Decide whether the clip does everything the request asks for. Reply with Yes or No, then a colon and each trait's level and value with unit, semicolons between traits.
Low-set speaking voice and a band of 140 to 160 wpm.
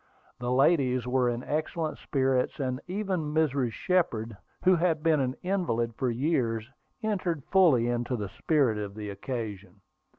Yes: low, 130 Hz; average, 145 wpm